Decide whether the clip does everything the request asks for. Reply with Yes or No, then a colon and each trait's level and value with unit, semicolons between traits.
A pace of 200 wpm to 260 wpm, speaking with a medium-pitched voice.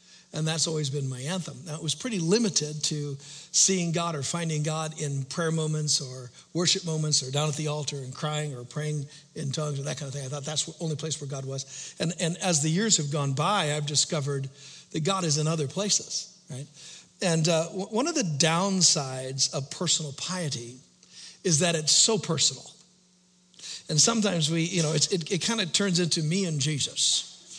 Yes: fast, 205 wpm; medium, 155 Hz